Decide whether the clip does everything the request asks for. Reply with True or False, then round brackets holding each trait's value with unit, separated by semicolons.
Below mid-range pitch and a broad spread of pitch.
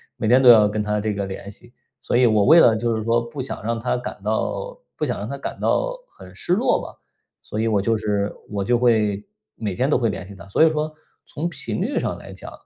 False (115 Hz; 3.4 semitones)